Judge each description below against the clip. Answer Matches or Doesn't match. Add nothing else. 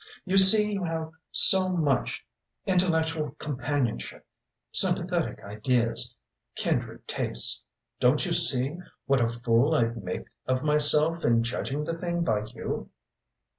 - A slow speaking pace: Matches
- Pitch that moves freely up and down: Matches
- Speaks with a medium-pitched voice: Matches